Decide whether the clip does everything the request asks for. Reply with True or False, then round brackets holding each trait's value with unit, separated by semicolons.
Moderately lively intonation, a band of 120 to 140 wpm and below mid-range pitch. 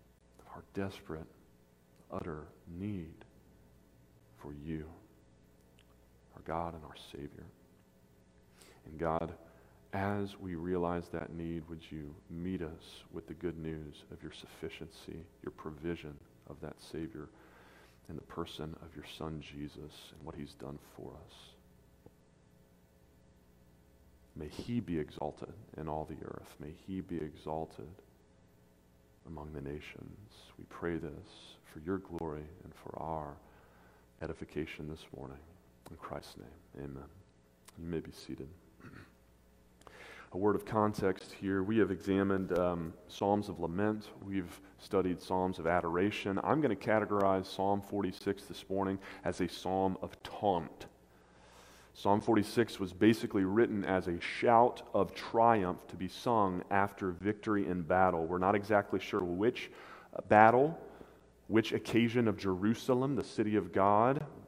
False (6.3 semitones; 135 wpm; 85 Hz)